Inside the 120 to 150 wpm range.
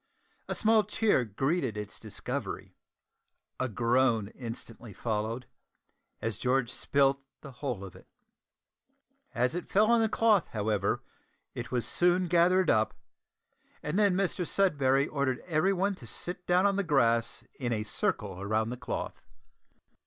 Yes: average, 140 wpm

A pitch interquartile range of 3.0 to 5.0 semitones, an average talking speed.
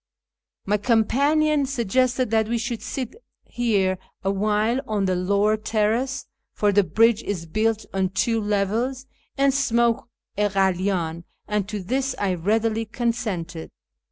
No: average, 3.3 semitones; slow, 130 wpm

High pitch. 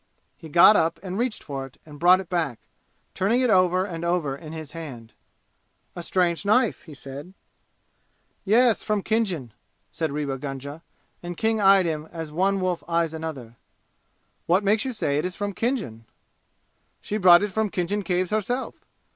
No: medium, 175 Hz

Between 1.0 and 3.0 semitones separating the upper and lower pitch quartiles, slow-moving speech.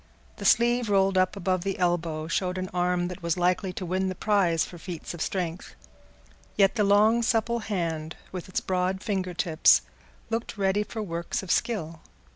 No: narrow, 2.6 semitones; average, 180 wpm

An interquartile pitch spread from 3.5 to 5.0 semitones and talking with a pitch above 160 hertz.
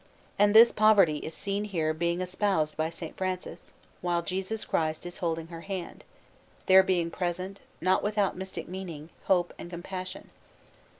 No: narrow, 2.4 semitones; medium, 185 Hz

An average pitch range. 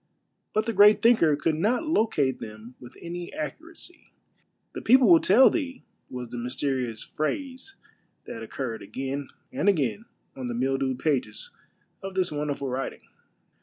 No: wide, 8.8 semitones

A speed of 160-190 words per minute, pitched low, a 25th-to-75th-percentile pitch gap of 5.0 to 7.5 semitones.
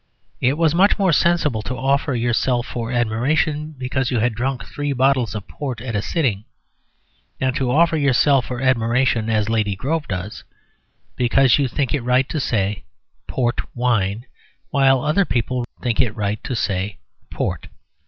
No: average, 165 wpm; low, 125 Hz; average, 3.6 semitones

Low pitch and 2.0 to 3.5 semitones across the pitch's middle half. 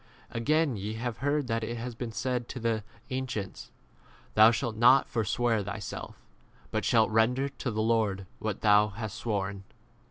Yes: low, 115 Hz; narrow, 2.4 semitones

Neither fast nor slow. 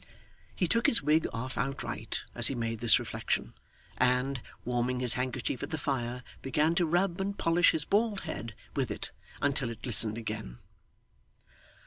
Yes: average, 160 wpm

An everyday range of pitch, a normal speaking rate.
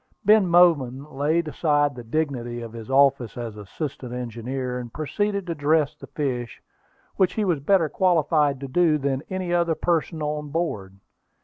Yes: average, 5.0 semitones; average, 165 wpm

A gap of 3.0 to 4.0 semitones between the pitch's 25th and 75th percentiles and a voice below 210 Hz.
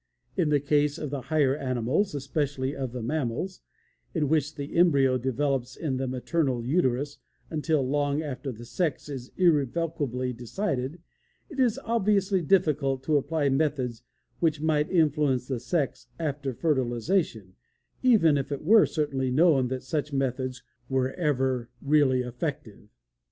Yes: average, 3.4 semitones; medium, 140 Hz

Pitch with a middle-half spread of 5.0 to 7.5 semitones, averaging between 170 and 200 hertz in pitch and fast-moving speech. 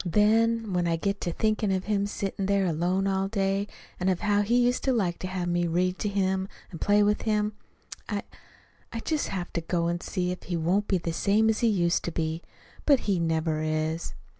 No: average, 3.2 semitones; high, 190 Hz; fast, 220 wpm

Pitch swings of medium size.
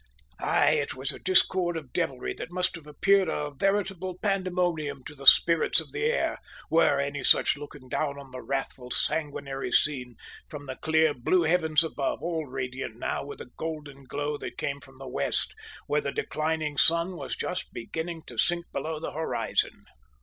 Yes: average, 3.6 semitones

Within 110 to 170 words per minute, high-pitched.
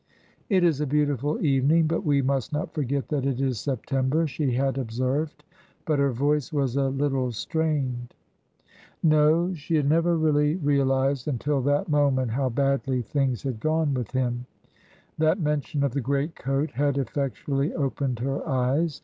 No: average, 160 wpm; medium, 140 Hz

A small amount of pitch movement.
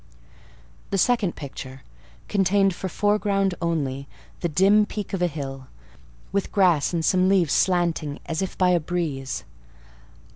No: average, 4.3 semitones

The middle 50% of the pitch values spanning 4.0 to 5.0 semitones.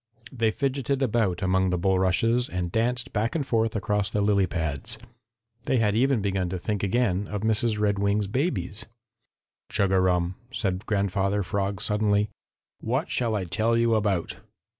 No: average, 3.1 semitones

